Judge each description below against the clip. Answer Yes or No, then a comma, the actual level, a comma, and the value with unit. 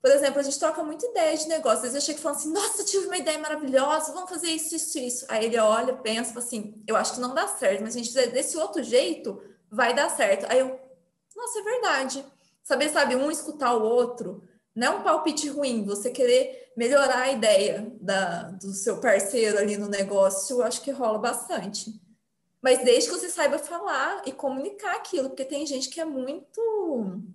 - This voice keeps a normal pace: No, fast, 205 wpm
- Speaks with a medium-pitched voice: No, very high, 270 Hz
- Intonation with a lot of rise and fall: Yes, wide, 6.3 semitones